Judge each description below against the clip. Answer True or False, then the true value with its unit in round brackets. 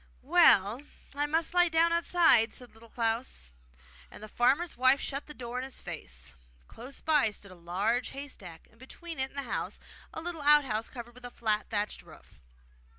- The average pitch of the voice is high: True (250 Hz)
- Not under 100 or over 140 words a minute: False (190 wpm)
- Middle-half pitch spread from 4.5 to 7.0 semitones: True (5.1 semitones)